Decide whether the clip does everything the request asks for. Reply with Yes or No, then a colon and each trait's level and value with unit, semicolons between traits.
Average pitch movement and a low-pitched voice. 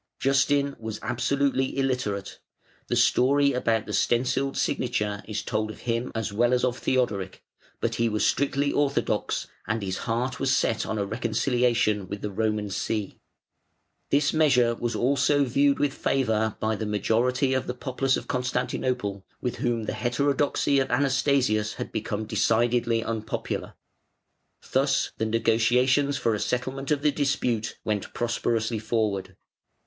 Yes: average, 3.6 semitones; low, 120 Hz